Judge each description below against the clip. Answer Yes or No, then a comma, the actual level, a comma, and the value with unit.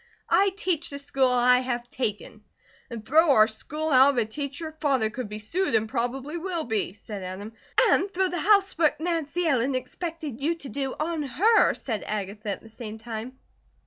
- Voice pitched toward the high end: Yes, very high, 265 Hz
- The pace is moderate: Yes, average, 185 wpm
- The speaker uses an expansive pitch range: Yes, wide, 6.5 semitones